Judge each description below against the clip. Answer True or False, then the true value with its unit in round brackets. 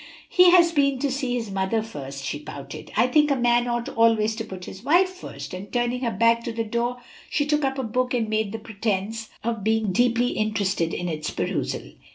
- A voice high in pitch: True (230 Hz)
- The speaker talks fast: True (215 wpm)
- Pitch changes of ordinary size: True (3.4 semitones)